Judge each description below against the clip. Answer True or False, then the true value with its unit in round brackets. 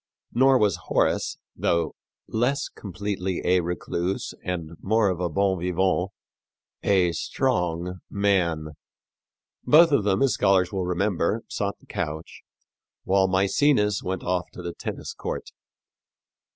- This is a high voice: False (95 Hz)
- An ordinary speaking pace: False (125 wpm)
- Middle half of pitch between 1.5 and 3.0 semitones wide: True (2.5 semitones)